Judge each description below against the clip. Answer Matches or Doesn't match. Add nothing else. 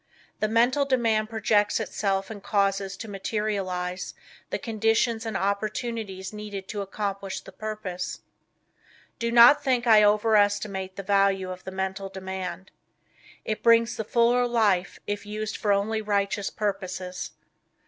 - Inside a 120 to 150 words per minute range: Matches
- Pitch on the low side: Doesn't match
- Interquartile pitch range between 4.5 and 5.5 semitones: Doesn't match